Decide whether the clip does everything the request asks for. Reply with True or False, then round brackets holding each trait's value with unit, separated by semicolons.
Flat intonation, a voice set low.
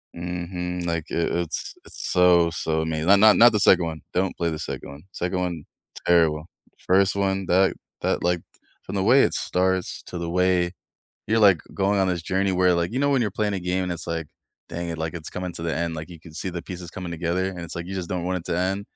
True (2.0 semitones; 90 Hz)